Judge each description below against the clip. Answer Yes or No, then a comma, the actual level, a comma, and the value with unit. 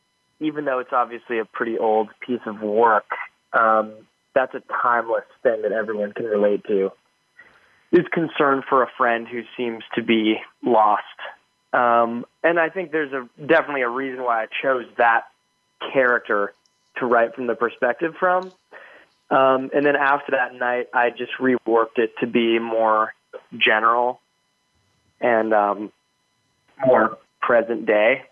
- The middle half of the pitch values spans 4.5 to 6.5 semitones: No, average, 3.3 semitones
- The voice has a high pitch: No, low, 120 Hz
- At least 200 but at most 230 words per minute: No, average, 145 wpm